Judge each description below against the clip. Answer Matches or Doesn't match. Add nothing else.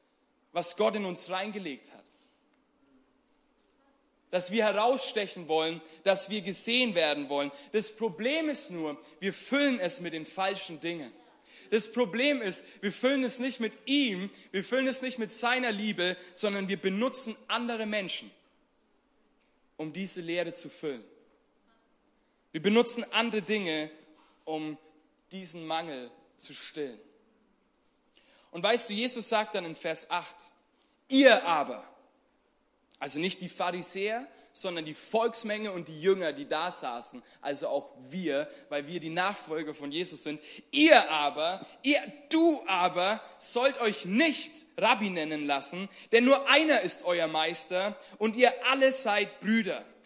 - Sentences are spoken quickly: Doesn't match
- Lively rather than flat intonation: Matches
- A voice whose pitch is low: Doesn't match